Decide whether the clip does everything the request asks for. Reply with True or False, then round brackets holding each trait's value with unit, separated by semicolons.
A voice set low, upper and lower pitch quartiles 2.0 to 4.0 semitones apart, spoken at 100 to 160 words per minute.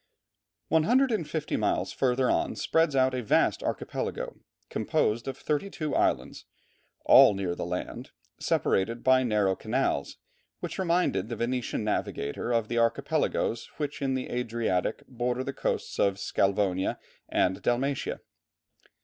False (120 Hz; 4.7 semitones; 140 wpm)